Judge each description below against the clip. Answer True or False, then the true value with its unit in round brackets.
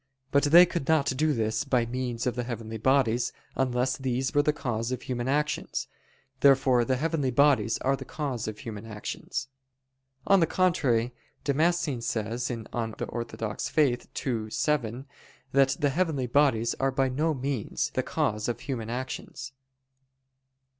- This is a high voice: False (130 Hz)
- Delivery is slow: False (155 wpm)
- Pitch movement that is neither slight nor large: True (3.3 semitones)